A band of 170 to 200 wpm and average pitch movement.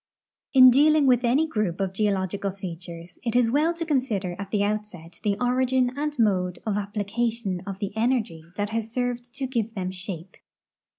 Yes: average, 175 wpm; average, 4.4 semitones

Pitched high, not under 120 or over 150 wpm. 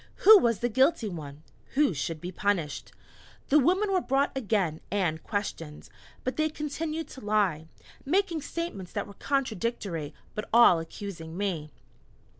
Yes: high, 210 Hz; average, 145 wpm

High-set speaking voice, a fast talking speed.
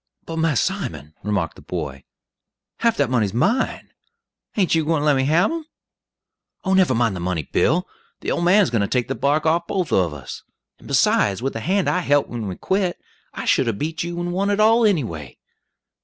No: medium, 150 Hz; fast, 210 wpm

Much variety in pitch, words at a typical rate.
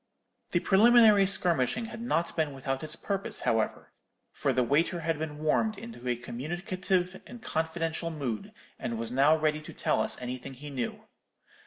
Yes: wide, 5.7 semitones; average, 165 wpm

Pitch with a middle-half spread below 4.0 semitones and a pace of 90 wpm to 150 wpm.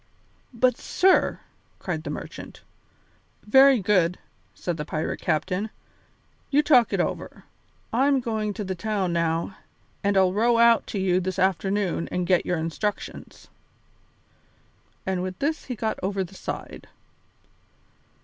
No: average, 4.3 semitones; average, 140 wpm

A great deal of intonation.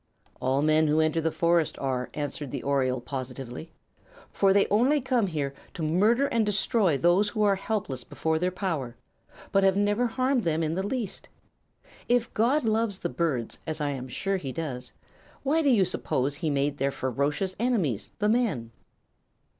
Yes: wide, 7.0 semitones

